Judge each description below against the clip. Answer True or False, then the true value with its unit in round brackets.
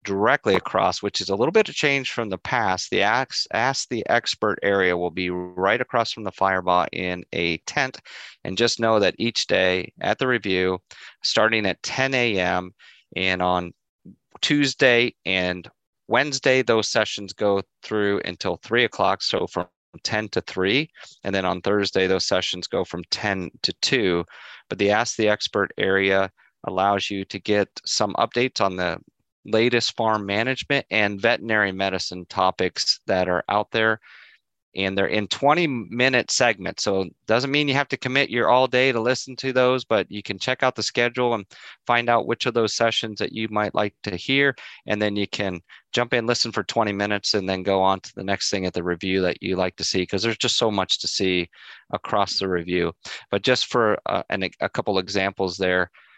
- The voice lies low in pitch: True (100 Hz)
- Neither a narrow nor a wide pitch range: True (4.1 semitones)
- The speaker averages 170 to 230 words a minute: True (190 wpm)